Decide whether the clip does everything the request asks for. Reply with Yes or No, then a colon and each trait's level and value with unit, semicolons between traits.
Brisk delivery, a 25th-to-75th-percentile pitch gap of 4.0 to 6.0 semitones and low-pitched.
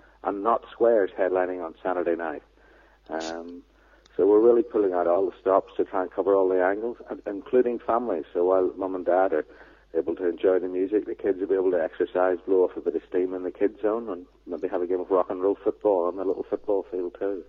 Yes: fast, 240 wpm; average, 4.7 semitones; very low, 95 Hz